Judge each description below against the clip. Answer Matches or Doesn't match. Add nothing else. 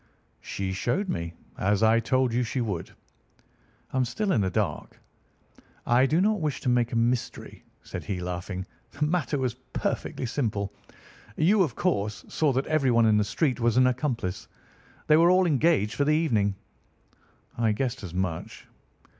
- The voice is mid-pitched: Doesn't match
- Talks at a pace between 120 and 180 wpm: Matches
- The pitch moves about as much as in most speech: Doesn't match